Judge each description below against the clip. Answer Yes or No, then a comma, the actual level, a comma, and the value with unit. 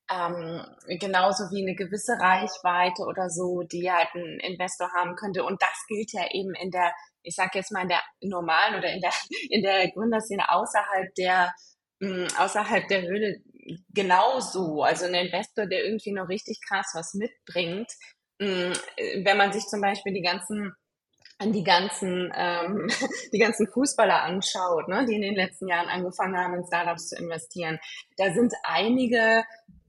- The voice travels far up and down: No, average, 2.8 semitones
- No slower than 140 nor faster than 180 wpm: Yes, average, 165 wpm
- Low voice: No, high, 190 Hz